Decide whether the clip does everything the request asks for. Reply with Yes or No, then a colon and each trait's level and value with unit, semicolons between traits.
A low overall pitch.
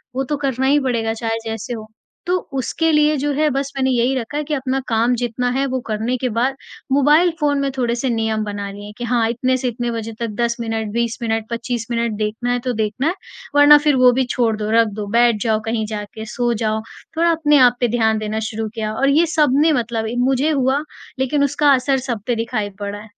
No: high, 240 Hz